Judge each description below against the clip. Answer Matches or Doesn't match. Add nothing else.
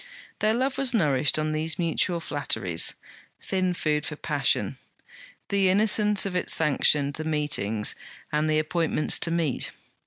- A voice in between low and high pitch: Matches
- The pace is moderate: Matches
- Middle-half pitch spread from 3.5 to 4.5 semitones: Matches